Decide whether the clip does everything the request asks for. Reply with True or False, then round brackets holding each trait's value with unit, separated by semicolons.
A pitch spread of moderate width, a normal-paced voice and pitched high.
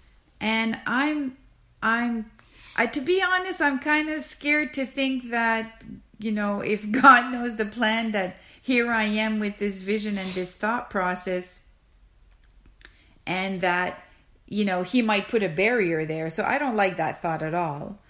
True (4.7 semitones; 165 wpm; 220 Hz)